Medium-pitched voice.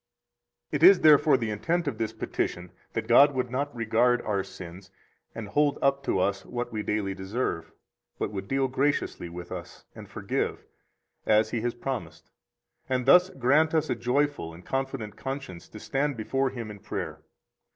No: low, 120 Hz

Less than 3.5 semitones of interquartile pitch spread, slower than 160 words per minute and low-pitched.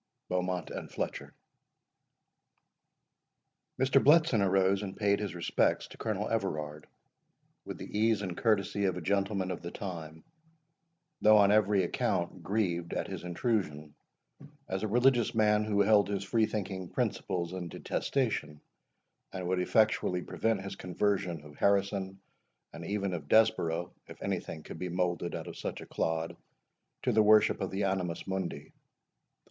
Yes: average, 3.1 semitones; average, 150 wpm; very low, 95 Hz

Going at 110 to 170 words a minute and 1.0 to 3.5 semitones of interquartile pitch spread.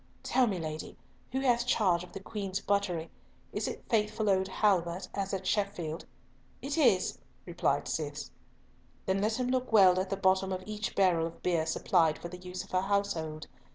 No: average, 185 wpm; average, 2.8 semitones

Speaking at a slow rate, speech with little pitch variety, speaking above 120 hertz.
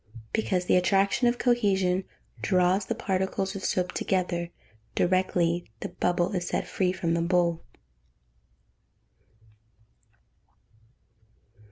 Yes: slow, 110 wpm; narrow, 1.6 semitones; medium, 185 Hz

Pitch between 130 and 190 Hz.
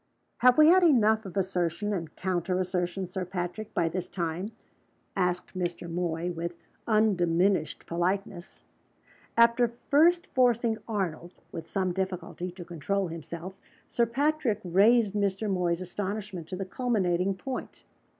Yes: medium, 185 Hz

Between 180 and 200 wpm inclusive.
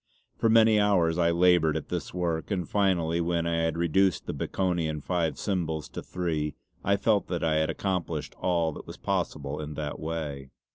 Yes: average, 185 wpm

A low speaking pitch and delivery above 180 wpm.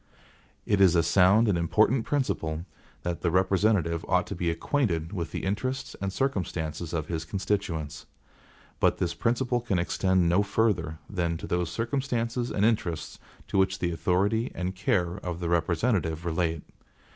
No: very low, 90 Hz; average, 155 wpm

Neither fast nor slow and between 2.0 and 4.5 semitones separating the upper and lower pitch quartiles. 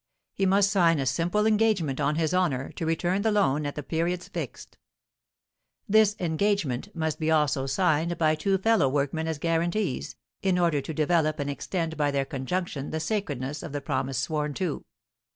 Yes: average, 175 wpm; average, 4.2 semitones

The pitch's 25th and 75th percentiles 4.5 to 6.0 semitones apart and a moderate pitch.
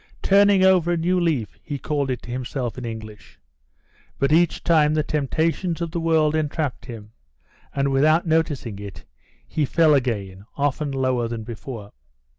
Yes: average, 5.1 semitones; medium, 145 Hz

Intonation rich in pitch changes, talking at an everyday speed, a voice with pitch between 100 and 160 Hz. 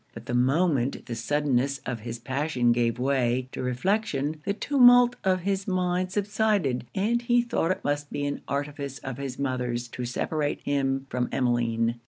Yes: wide, 6.8 semitones; average, 170 wpm; medium, 140 Hz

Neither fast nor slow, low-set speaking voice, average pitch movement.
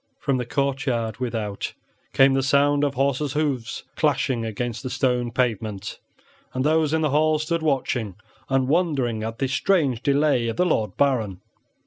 Yes: average, 160 wpm; low, 130 Hz; average, 3.7 semitones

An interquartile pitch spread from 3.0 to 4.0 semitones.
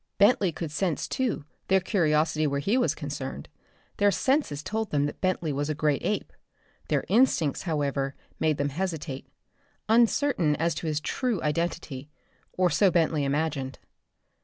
No: average, 4.9 semitones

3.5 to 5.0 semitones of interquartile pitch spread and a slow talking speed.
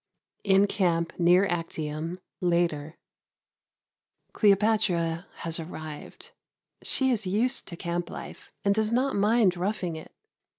Yes: average, 3.8 semitones; slow, 115 wpm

